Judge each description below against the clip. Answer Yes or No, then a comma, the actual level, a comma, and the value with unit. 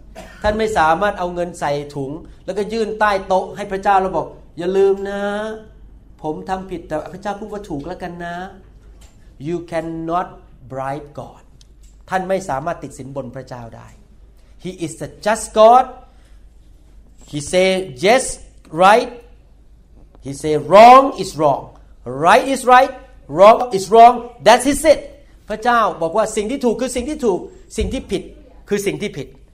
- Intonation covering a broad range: Yes, wide, 6.0 semitones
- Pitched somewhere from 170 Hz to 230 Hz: Yes, medium, 185 Hz